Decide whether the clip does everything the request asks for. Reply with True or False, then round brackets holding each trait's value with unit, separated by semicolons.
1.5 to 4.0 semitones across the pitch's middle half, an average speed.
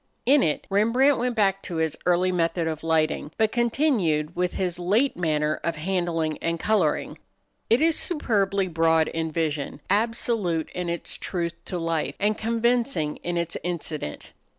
False (5.2 semitones; 155 wpm)